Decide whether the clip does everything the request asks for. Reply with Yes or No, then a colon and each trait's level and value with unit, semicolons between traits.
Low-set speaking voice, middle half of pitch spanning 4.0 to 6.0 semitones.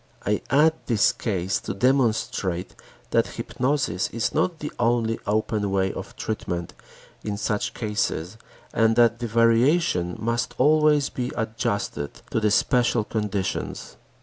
No: low, 115 Hz; average, 3.3 semitones